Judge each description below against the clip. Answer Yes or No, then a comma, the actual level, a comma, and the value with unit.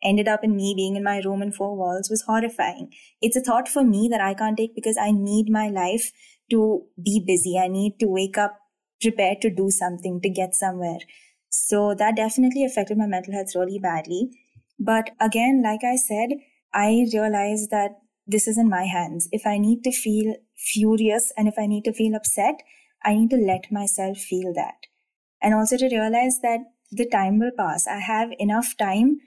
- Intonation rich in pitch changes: No, narrow, 2.5 semitones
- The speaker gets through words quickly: Yes, fast, 200 wpm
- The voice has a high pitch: Yes, high, 215 Hz